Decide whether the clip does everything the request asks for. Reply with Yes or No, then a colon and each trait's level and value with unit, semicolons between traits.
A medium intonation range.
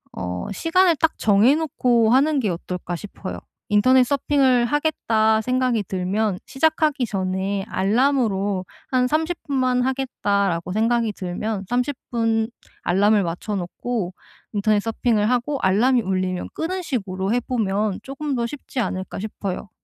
Yes: average, 4.9 semitones